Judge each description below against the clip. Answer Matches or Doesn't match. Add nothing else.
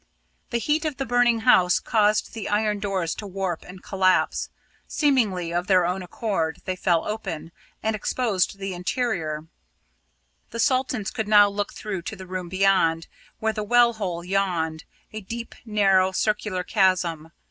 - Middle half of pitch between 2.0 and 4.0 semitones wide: Matches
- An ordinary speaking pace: Matches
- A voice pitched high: Matches